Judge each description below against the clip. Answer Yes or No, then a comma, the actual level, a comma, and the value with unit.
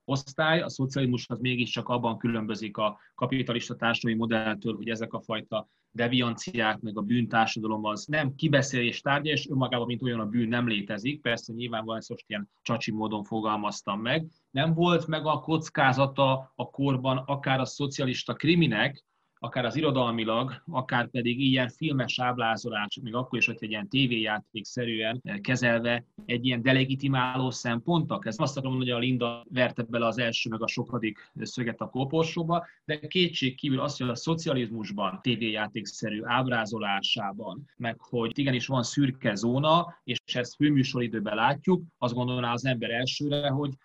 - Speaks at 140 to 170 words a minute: Yes, average, 150 wpm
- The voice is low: Yes, low, 125 Hz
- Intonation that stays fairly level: No, average, 3.0 semitones